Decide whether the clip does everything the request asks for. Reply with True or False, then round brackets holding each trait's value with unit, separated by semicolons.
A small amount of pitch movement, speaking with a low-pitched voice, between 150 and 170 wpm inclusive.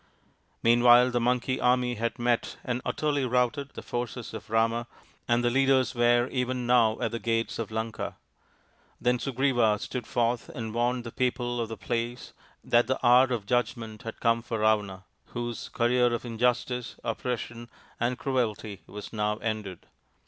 True (1.5 semitones; 120 Hz; 160 wpm)